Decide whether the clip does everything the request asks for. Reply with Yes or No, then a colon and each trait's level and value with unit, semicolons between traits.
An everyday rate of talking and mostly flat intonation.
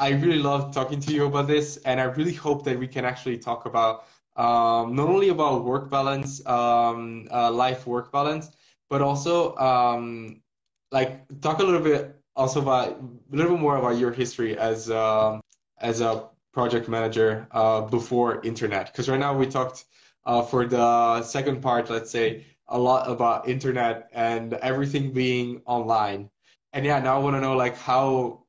No: average, 175 wpm; average, 3.0 semitones